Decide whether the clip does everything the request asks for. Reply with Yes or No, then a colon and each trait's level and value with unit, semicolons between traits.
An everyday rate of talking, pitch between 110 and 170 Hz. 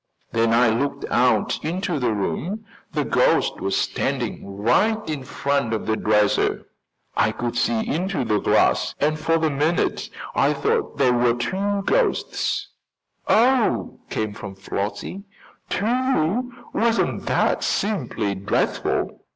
No: slow, 130 wpm; medium, 140 Hz